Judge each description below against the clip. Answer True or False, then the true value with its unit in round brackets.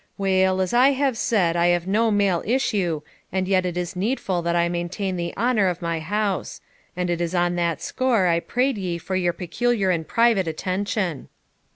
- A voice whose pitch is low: False (185 Hz)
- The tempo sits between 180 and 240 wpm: True (195 wpm)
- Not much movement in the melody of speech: False (3.3 semitones)